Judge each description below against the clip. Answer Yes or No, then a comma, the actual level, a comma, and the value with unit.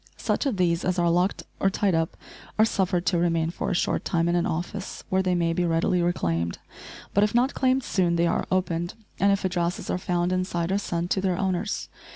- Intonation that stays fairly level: Yes, narrow, 2.0 semitones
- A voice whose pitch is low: No, medium, 180 Hz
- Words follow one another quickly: Yes, fast, 220 wpm